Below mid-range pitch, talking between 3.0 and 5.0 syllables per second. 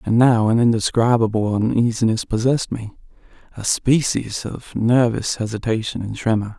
Yes: low, 115 Hz; 4.9 syllables/s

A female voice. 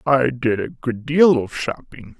No: male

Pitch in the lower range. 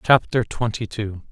Yes: low, 110 Hz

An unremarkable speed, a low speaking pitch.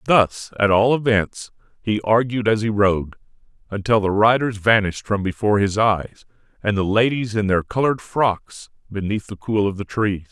Yes: average, 175 wpm; low, 105 Hz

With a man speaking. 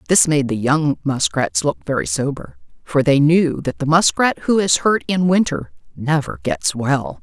No: female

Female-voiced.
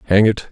No: male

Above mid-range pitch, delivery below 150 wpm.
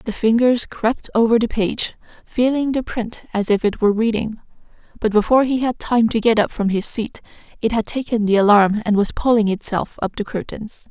No: high, 225 Hz; fast, 205 wpm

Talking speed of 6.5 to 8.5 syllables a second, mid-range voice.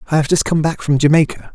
Yes: 6.8 syllables/s; medium, 150 Hz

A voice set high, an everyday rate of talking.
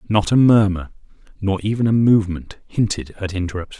No: low, 100 Hz; average, 160 wpm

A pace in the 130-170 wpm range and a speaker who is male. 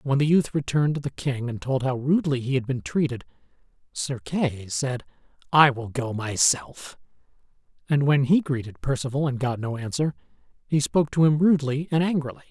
No: average, 185 wpm; male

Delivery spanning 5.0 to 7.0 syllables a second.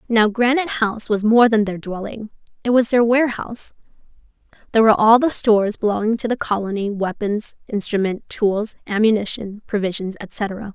Yes: 5.5 syllables/s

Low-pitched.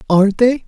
No: high, 220 Hz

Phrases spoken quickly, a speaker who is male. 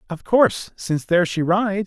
No: average, 195 wpm; male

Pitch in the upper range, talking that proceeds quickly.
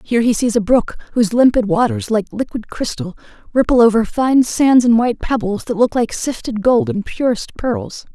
No: high, 235 Hz; average, 190 wpm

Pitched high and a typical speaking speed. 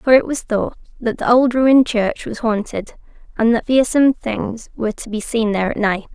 No: high, 230 Hz; fast, 215 wpm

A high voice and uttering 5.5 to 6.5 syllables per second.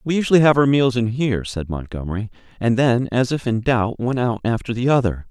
No: low, 120 Hz; 5.8 syllables/s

